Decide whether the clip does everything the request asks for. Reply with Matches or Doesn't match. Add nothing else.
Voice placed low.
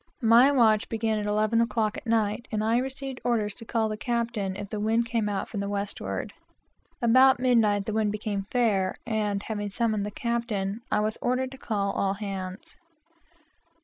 Doesn't match